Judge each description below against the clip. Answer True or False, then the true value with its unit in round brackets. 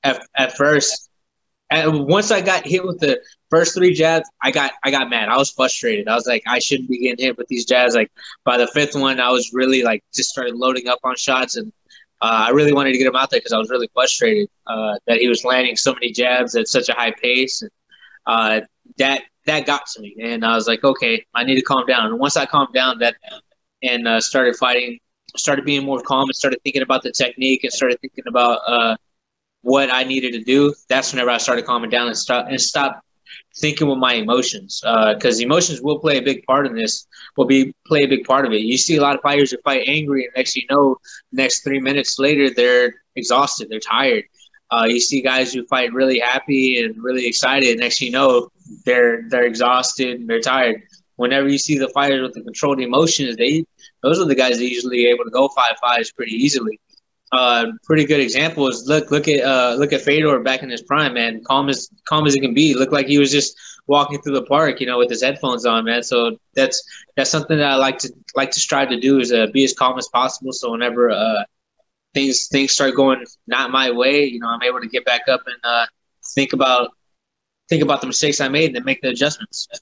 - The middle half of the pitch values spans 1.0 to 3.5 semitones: True (2.7 semitones)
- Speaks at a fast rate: True (240 wpm)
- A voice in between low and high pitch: False (130 Hz)